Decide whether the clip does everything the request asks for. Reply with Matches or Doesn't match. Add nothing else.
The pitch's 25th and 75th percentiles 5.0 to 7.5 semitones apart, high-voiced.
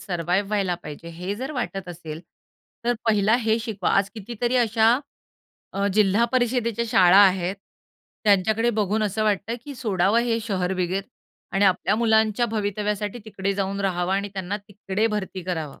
Doesn't match